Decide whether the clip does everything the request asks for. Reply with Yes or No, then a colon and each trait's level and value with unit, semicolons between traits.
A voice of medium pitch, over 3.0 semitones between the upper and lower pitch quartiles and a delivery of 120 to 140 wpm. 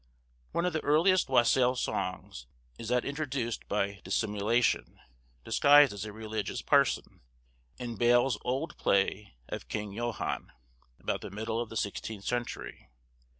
No: low, 120 Hz; average, 3.8 semitones; slow, 135 wpm